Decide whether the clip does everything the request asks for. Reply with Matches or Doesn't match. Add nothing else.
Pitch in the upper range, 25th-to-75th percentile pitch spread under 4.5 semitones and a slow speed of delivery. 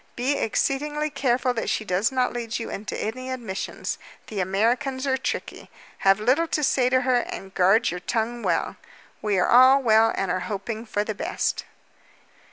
Doesn't match